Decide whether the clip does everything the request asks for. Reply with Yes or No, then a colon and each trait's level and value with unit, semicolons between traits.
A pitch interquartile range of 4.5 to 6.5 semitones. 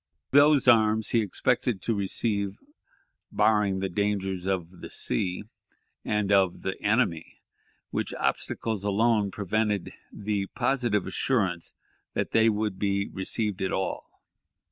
No: narrow, 2.5 semitones